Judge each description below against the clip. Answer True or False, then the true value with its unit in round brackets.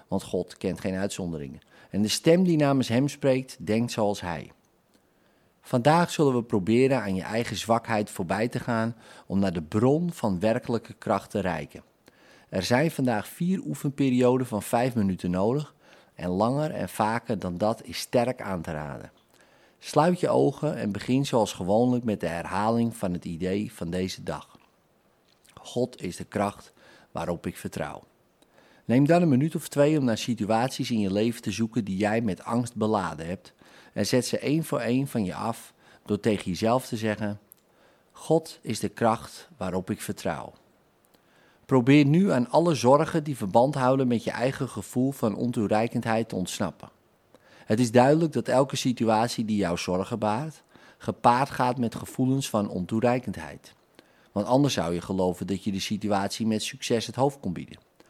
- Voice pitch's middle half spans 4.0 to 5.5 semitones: True (4.3 semitones)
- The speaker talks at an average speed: True (170 wpm)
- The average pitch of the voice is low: True (115 Hz)